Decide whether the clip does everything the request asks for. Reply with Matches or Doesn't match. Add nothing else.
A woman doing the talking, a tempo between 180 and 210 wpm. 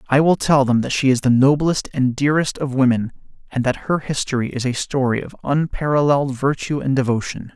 Doesn't match